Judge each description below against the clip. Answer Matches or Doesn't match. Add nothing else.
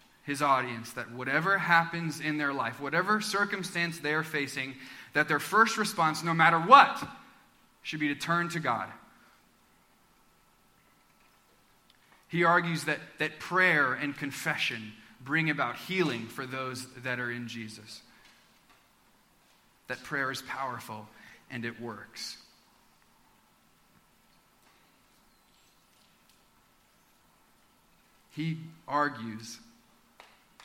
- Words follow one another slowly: Matches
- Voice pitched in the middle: Matches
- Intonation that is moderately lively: Matches